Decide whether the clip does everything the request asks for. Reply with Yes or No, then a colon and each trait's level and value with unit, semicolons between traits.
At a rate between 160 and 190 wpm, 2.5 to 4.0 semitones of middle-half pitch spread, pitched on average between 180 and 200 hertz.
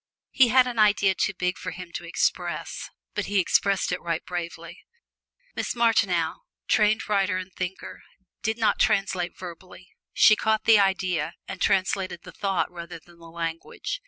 Yes: average, 165 wpm; average, 2.9 semitones; medium, 185 Hz